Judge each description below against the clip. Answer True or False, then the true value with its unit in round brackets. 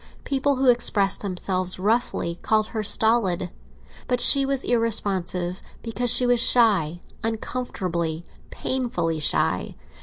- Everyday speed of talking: False (115 wpm)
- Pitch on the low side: False (215 Hz)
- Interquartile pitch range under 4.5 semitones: False (5.2 semitones)